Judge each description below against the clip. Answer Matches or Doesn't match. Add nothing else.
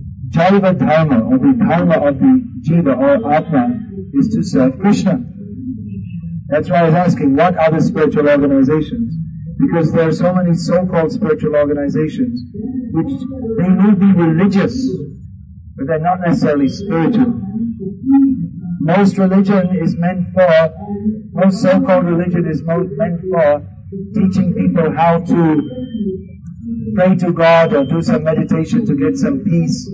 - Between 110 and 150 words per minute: Matches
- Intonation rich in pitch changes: Doesn't match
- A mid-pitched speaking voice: Matches